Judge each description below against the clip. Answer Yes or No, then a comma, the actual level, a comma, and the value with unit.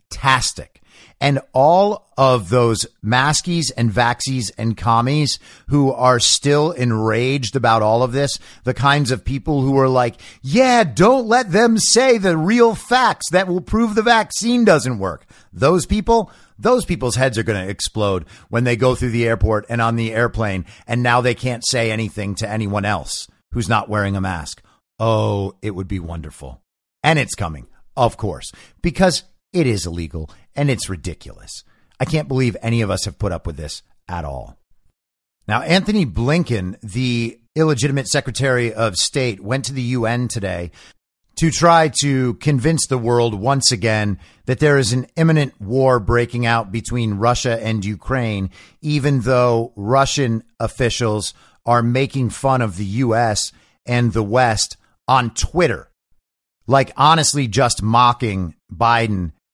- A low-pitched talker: Yes, low, 120 Hz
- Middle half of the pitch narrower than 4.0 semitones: No, average, 4.6 semitones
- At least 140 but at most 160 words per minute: Yes, average, 155 wpm